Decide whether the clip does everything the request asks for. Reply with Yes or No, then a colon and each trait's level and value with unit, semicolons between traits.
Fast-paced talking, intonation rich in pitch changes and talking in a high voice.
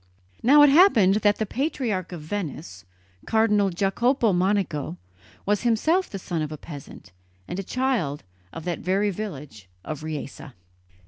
No: average, 145 wpm; wide, 6.2 semitones; high, 195 Hz